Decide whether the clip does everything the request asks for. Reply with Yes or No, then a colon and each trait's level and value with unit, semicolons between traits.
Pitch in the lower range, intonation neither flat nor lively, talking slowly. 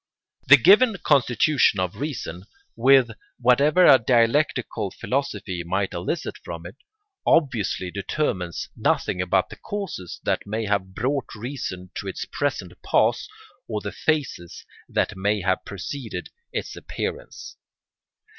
No: low, 115 Hz; wide, 7.1 semitones; slow, 125 wpm